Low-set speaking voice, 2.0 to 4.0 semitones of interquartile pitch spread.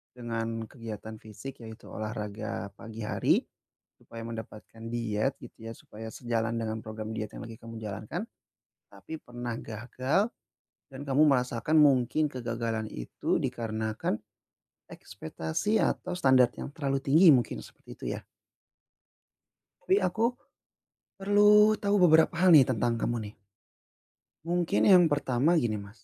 No: low, 120 Hz; average, 4.8 semitones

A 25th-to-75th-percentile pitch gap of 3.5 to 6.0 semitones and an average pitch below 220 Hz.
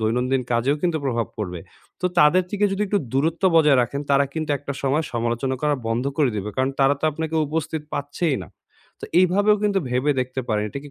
Yes: average, 4.5 semitones; medium, 140 Hz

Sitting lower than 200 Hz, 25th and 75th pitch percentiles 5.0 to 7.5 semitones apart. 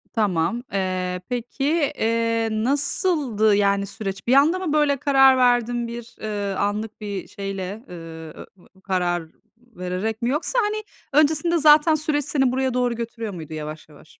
No: high, 230 Hz; wide, 5.6 semitones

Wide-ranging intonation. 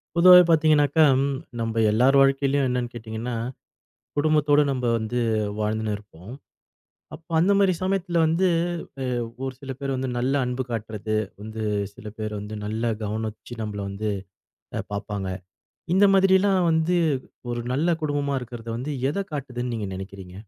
Yes: wide, 5.8 semitones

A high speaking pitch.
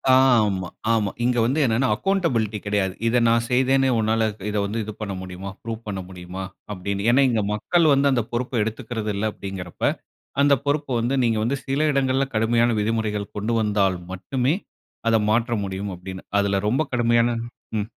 No: low, 115 Hz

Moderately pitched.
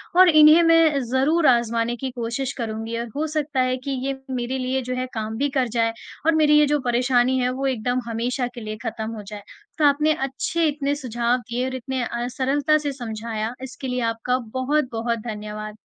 No: very high, 255 Hz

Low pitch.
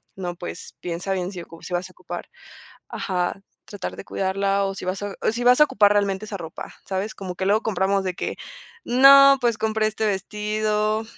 No: high, 200 Hz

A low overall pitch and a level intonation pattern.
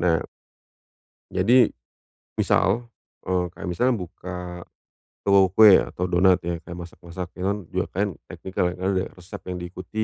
Yes: very low, 95 Hz; narrow, 2.0 semitones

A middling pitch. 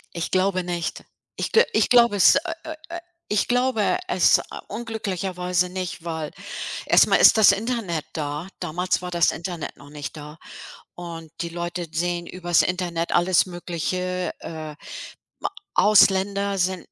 Yes: medium, 180 Hz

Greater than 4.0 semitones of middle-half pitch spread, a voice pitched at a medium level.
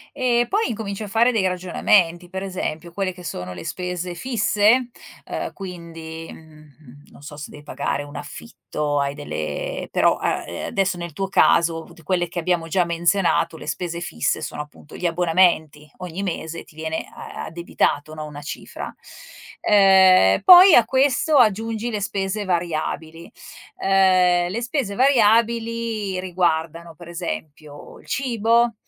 Yes: average, 4.7 semitones; medium, 180 Hz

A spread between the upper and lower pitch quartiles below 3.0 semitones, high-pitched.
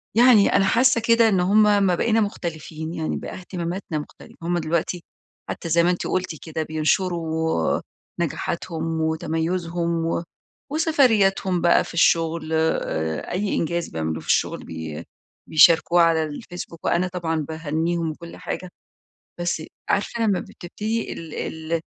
No: narrow, 2.6 semitones; medium, 170 Hz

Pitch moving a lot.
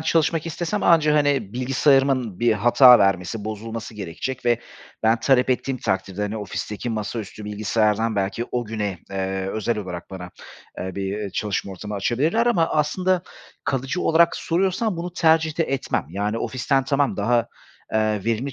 Yes: wide, 5.7 semitones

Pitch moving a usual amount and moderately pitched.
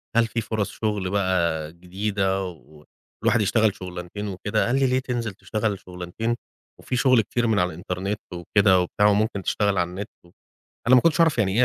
No: average, 3.5 semitones; low, 100 Hz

